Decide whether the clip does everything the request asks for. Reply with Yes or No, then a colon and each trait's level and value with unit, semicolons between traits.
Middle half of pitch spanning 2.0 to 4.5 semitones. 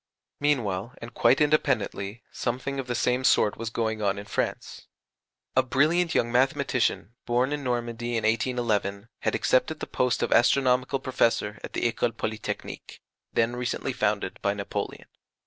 Yes: average, 2.7 semitones